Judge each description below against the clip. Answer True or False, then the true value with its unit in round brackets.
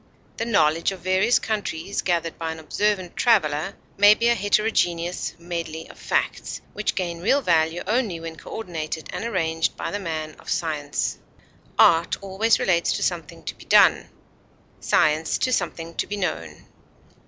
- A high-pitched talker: False (175 Hz)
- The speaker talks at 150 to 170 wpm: True (155 wpm)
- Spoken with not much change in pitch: False (4.1 semitones)